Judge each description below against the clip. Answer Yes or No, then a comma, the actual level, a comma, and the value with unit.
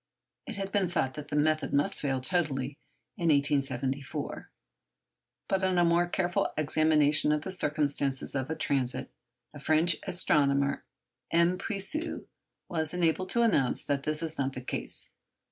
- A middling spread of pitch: Yes, average, 3.8 semitones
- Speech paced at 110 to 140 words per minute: No, average, 150 wpm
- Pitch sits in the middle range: Yes, medium, 155 Hz